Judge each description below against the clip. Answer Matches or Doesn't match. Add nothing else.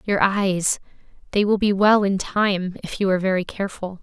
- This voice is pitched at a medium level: Doesn't match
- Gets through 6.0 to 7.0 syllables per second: Doesn't match